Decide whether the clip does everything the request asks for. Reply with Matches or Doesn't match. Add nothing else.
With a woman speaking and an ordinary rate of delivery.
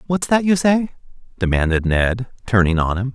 Doesn't match